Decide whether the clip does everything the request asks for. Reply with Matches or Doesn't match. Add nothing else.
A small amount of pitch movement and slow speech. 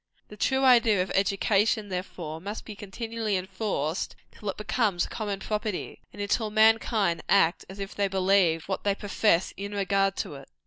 Doesn't match